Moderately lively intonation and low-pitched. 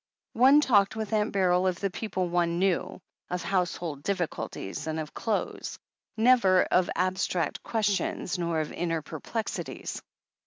No: average, 3.4 semitones; medium, 185 Hz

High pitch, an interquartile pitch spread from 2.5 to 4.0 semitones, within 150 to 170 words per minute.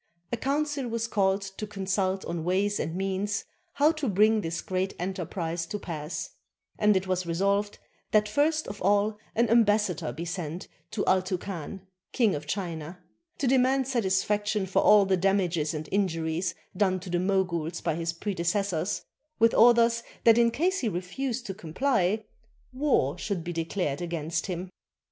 Yes: high, 195 Hz; average, 3.7 semitones; average, 160 wpm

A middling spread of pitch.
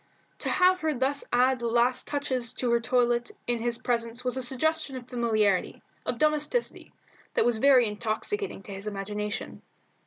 Yes: average, 3.0 semitones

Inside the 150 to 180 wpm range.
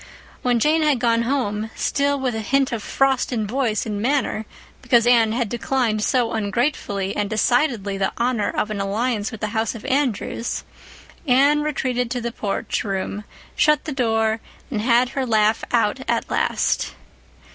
Yes: average, 160 wpm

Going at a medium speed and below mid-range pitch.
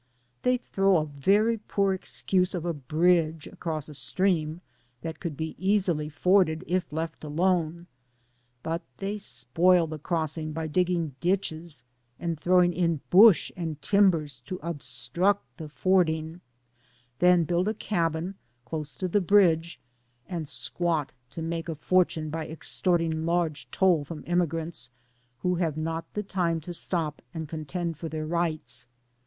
No: average, 145 wpm; medium, 165 Hz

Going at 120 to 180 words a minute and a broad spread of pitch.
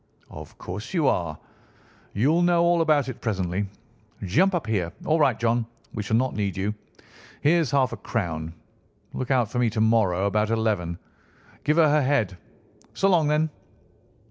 Yes: average, 170 wpm; wide, 7.1 semitones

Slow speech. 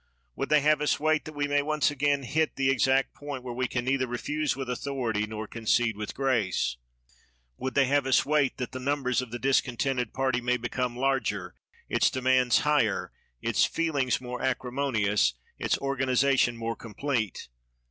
No: average, 170 wpm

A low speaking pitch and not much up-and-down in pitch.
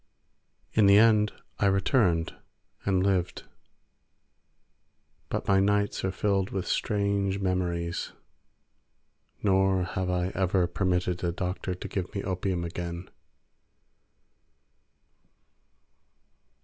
Yes: very low, 95 Hz; narrow, 1.7 semitones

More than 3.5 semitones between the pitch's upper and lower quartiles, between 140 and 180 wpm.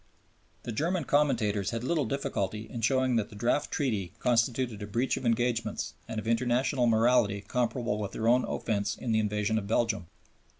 No: average, 2.8 semitones; average, 175 wpm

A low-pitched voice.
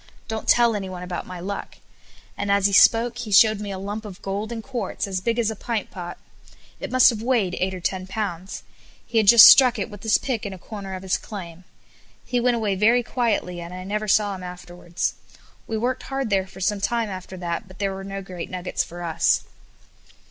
No: high, 200 Hz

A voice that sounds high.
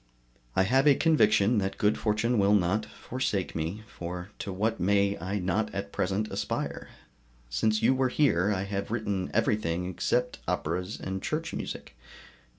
No: low, 100 Hz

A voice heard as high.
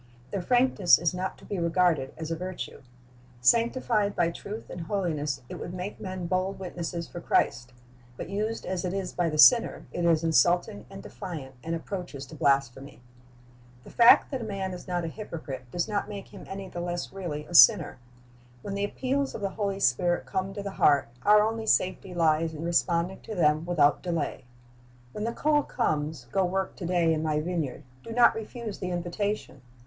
No: medium, 180 Hz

